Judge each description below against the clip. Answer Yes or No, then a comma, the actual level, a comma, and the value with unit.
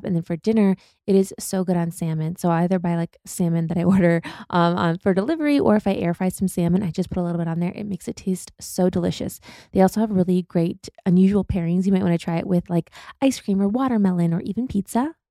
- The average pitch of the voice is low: No, medium, 185 Hz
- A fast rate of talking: Yes, fast, 260 wpm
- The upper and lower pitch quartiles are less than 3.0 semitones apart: Yes, narrow, 2.4 semitones